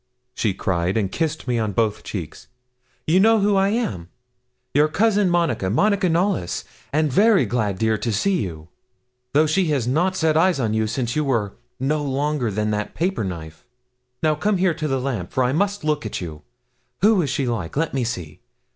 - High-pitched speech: No, low, 135 Hz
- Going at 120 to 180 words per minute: No, average, 195 wpm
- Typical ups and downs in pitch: No, wide, 8.4 semitones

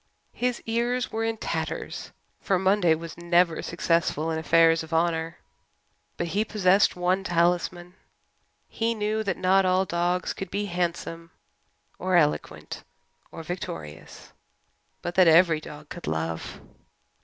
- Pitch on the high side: No, medium, 175 Hz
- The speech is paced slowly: Yes, slow, 130 wpm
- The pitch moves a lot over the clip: No, average, 2.7 semitones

